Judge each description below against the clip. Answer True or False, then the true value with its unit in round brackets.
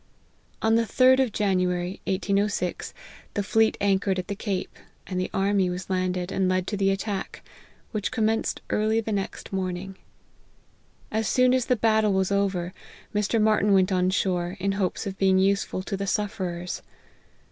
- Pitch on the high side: True (195 Hz)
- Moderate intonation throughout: False (2.3 semitones)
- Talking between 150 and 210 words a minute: True (170 wpm)